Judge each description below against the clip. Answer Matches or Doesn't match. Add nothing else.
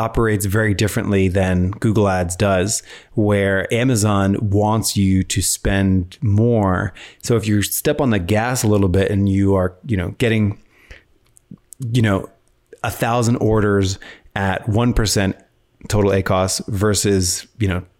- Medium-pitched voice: Doesn't match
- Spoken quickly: Doesn't match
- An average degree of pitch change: Doesn't match